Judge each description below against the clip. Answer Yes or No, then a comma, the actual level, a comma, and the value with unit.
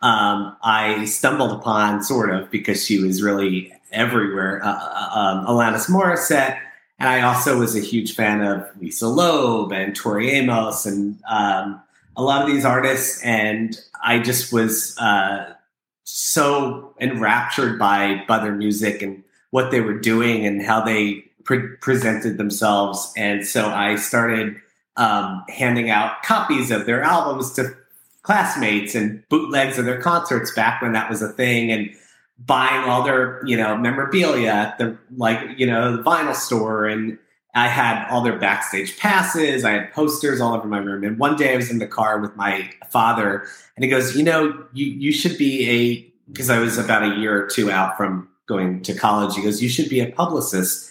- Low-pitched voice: Yes, low, 110 Hz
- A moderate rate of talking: Yes, average, 180 wpm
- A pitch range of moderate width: Yes, average, 3.7 semitones